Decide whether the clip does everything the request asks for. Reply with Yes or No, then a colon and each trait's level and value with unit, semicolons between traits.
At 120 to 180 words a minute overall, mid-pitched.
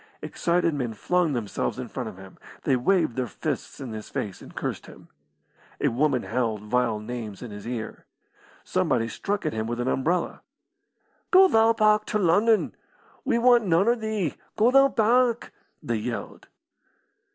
Yes: average, 165 wpm; medium, 150 Hz